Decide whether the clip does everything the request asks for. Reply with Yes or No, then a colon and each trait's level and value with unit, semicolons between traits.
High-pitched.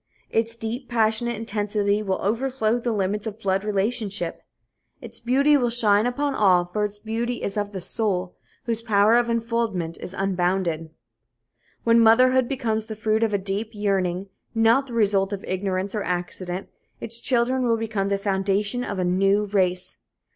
Yes: high, 210 Hz